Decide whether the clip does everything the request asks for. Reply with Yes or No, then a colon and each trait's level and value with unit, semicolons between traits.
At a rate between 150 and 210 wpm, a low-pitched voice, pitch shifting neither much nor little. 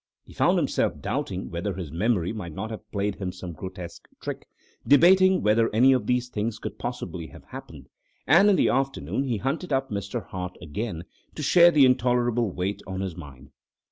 No: average, 185 wpm; low, 110 Hz; wide, 6.1 semitones